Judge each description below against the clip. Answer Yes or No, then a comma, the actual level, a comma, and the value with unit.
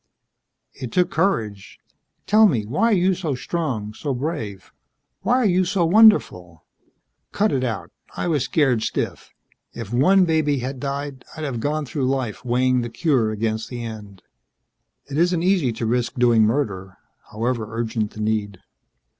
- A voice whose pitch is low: Yes, low, 130 Hz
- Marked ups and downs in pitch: Yes, wide, 6.5 semitones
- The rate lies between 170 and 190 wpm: No, average, 160 wpm